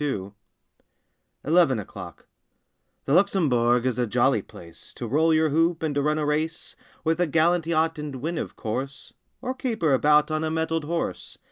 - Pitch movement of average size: Yes, average, 3.3 semitones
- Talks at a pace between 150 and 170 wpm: No, average, 195 wpm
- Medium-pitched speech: Yes, medium, 155 Hz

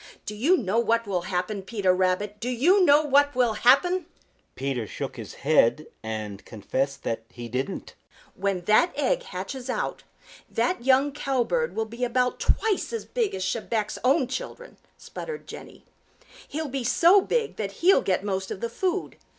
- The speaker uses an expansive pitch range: Yes, wide, 8.0 semitones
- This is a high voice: Yes, high, 235 Hz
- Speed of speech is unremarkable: Yes, average, 165 wpm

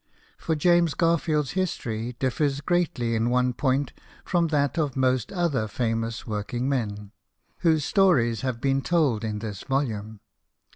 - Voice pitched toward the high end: No, low, 130 Hz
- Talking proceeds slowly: No, average, 145 wpm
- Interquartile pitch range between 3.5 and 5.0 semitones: No, wide, 5.4 semitones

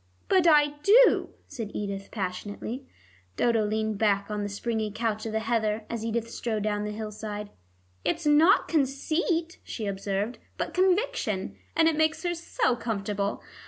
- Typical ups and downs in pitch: No, wide, 6.3 semitones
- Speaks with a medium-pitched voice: No, high, 225 Hz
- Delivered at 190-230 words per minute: No, average, 155 wpm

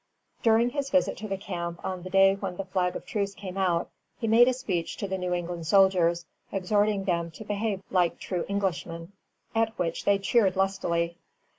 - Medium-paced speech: Yes, average, 195 wpm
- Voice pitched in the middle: No, high, 195 Hz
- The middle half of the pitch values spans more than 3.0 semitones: No, narrow, 2.6 semitones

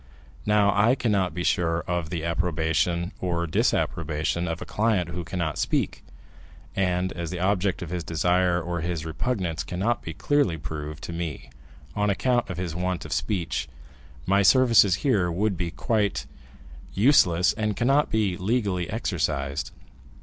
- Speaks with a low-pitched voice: Yes, very low, 90 Hz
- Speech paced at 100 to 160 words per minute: Yes, average, 150 wpm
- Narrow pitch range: No, average, 3.5 semitones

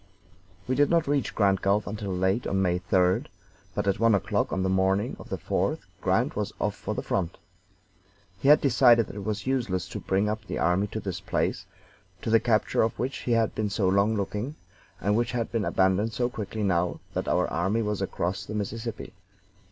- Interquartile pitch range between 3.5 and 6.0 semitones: No, average, 3.1 semitones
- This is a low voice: Yes, low, 105 Hz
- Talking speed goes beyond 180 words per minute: Yes, fast, 205 wpm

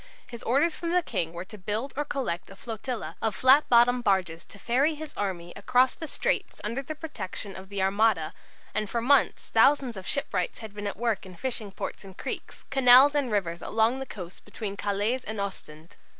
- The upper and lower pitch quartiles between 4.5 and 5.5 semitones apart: Yes, average, 5.1 semitones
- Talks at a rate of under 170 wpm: No, average, 200 wpm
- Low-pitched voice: No, high, 220 Hz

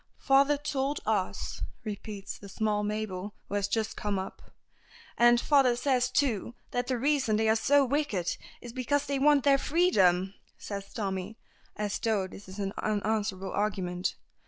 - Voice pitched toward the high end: Yes, high, 220 Hz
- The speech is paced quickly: No, average, 160 wpm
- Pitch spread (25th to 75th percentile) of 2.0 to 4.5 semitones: No, average, 5.2 semitones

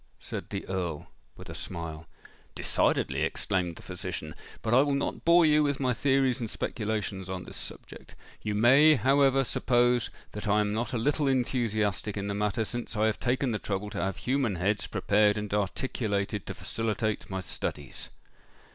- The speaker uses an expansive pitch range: No, average, 4.2 semitones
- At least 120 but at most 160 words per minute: No, average, 175 wpm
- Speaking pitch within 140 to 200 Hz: No, low, 110 Hz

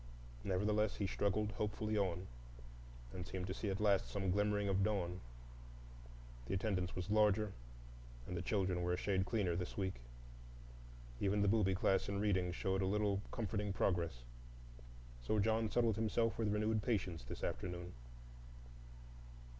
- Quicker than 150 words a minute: No, average, 145 wpm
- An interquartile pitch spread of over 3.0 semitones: No, narrow, 2.5 semitones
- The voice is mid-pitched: No, low, 100 Hz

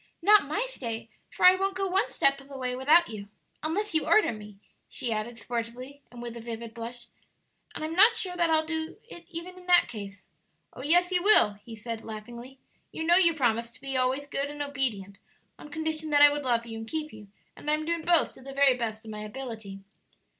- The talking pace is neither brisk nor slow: No, fast, 225 wpm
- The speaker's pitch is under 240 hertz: No, very high, 275 Hz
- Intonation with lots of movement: Yes, wide, 6.0 semitones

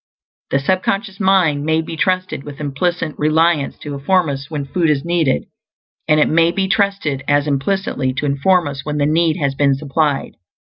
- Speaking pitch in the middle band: Yes, medium, 155 Hz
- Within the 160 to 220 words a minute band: Yes, average, 185 wpm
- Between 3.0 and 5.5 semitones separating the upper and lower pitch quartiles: Yes, average, 3.7 semitones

